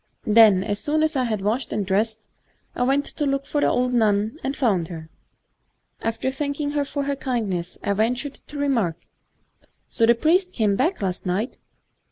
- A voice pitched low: No, high, 235 Hz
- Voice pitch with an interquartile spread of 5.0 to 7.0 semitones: Yes, wide, 5.5 semitones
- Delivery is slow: No, average, 190 wpm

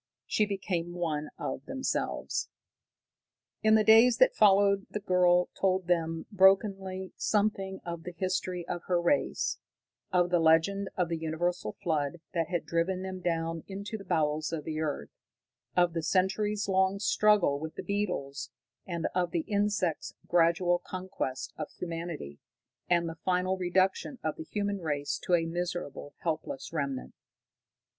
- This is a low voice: No, medium, 180 Hz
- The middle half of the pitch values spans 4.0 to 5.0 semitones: No, average, 2.8 semitones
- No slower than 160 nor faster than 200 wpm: No, average, 150 wpm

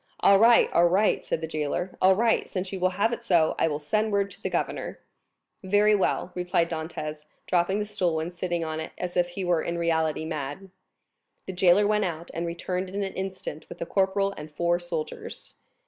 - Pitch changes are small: No, average, 3.1 semitones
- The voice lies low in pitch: No, medium, 180 Hz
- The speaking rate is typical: No, fast, 210 wpm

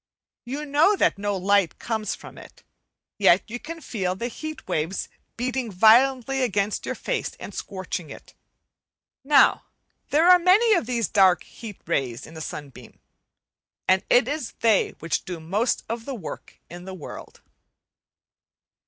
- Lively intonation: Yes, wide, 6.2 semitones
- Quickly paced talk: No, average, 155 wpm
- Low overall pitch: No, high, 220 Hz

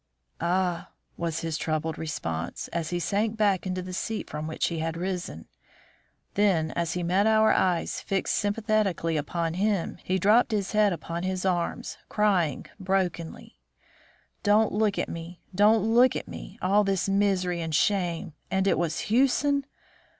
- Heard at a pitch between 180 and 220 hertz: Yes, medium, 185 Hz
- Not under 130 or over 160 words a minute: Yes, average, 155 wpm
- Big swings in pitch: No, average, 3.6 semitones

